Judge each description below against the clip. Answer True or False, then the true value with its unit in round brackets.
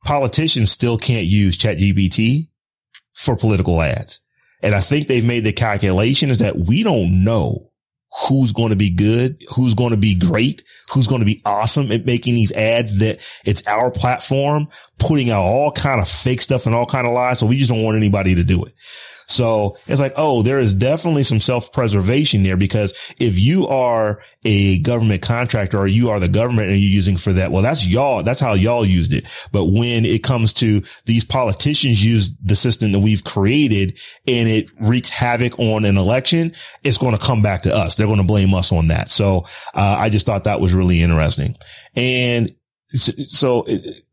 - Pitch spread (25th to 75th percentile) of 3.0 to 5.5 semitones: True (3.9 semitones)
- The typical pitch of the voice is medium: False (115 Hz)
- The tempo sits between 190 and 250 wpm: True (200 wpm)